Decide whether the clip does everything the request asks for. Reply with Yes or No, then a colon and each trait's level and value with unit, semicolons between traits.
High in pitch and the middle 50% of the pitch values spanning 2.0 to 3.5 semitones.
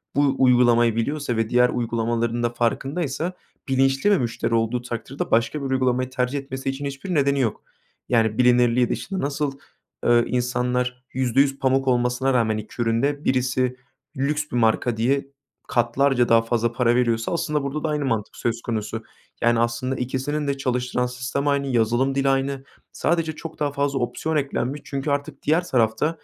No: low, 130 Hz; average, 2.8 semitones